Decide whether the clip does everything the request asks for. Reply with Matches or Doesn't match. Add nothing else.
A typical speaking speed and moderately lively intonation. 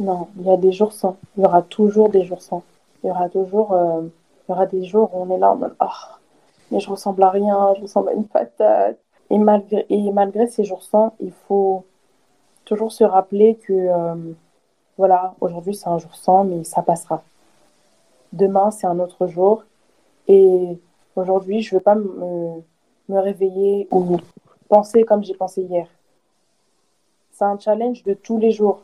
Doesn't match